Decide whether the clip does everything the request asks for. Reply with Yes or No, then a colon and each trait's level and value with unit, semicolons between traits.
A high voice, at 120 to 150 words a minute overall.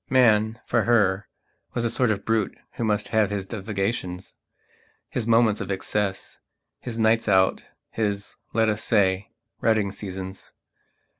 No: low, 105 Hz; average, 140 wpm